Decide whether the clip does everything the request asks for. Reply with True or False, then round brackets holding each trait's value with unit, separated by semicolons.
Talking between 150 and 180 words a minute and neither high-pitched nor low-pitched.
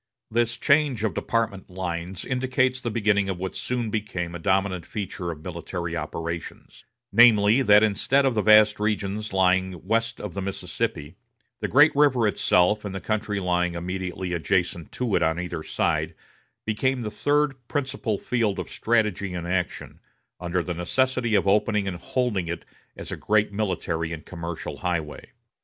False (160 wpm; 100 Hz)